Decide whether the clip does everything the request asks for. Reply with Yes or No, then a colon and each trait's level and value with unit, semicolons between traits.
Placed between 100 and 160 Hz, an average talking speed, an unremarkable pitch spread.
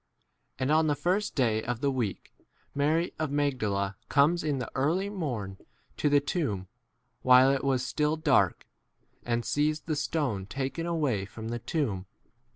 Yes: medium, 140 Hz; average, 160 wpm; average, 4.8 semitones